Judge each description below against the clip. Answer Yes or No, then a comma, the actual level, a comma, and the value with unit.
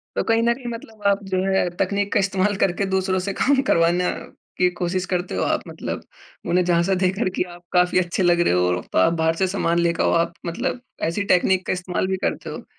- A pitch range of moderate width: No, narrow, 2.3 semitones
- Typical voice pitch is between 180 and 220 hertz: Yes, medium, 185 Hz